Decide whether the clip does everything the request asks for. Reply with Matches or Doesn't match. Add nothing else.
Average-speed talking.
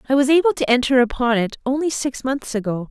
Doesn't match